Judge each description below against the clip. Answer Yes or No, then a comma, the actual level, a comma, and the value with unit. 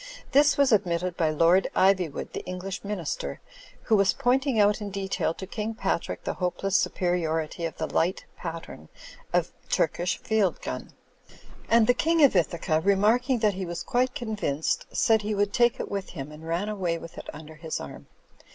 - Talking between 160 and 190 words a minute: Yes, average, 180 wpm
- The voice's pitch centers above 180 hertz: Yes, high, 190 Hz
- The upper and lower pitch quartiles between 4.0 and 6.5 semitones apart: Yes, average, 4.4 semitones